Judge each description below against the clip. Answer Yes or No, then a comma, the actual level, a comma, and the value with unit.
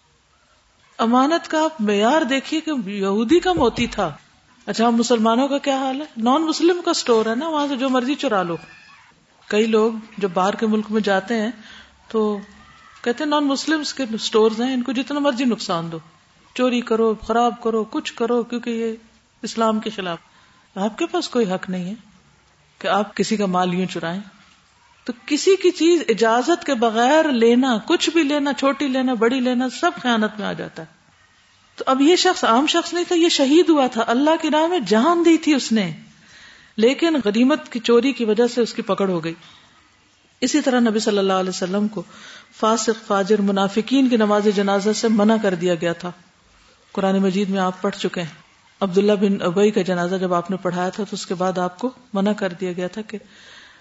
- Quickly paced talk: Yes, fast, 200 wpm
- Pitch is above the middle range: Yes, high, 225 Hz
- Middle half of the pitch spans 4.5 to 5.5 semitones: Yes, average, 5.1 semitones